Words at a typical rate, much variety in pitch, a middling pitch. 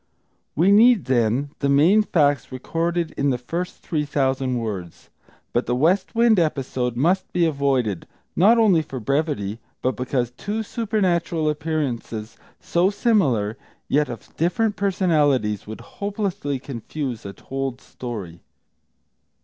No: slow, 130 wpm; wide, 6.3 semitones; medium, 145 Hz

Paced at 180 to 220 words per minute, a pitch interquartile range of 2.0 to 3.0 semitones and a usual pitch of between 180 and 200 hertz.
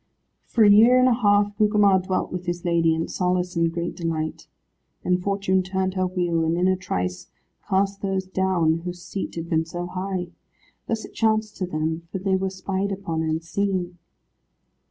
Yes: average, 185 wpm; narrow, 2.6 semitones; medium, 185 Hz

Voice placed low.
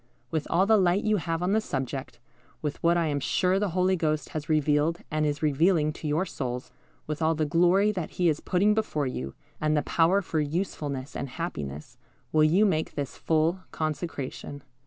No: medium, 160 Hz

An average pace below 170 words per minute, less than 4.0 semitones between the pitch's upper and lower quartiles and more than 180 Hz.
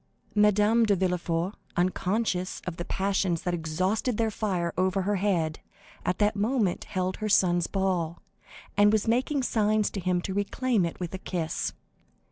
Yes: average, 160 wpm; average, 2.9 semitones; high, 190 Hz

